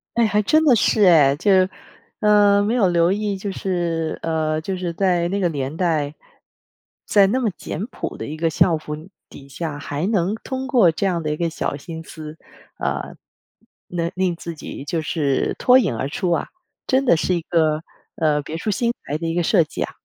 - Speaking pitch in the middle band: Yes, medium, 170 Hz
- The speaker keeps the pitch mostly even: No, average, 4.4 semitones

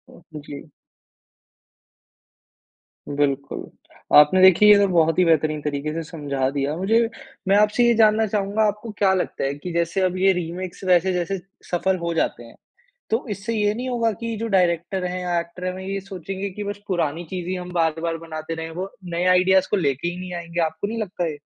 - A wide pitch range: No, average, 3.2 semitones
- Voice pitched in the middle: Yes, medium, 180 Hz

